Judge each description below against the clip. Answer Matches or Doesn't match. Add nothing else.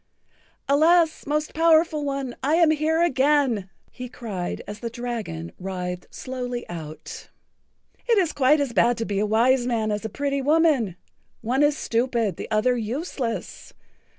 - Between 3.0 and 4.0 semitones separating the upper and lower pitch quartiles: Doesn't match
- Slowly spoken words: Doesn't match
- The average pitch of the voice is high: Matches